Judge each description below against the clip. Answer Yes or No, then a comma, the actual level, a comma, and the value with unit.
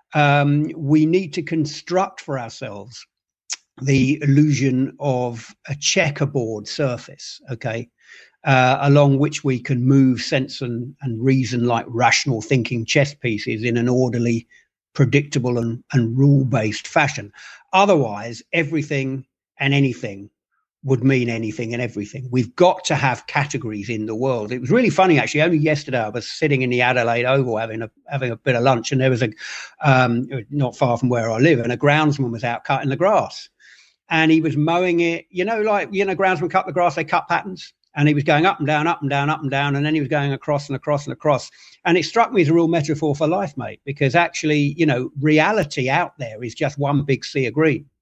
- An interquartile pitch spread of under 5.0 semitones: Yes, average, 3.8 semitones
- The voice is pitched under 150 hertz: Yes, medium, 140 Hz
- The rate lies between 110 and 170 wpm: No, average, 200 wpm